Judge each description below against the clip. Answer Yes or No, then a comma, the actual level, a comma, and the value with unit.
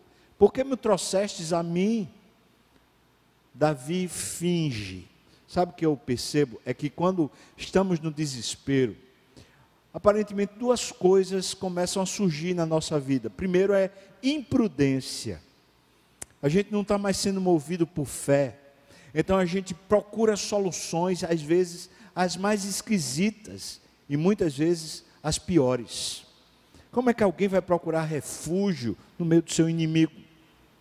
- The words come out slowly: No, average, 130 wpm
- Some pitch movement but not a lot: No, wide, 5.7 semitones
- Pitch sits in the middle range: Yes, medium, 175 Hz